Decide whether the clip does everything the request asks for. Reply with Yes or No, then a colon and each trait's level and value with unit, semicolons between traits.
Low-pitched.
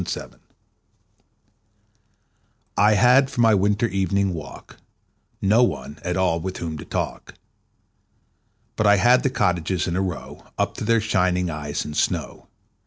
Yes: very low, 95 Hz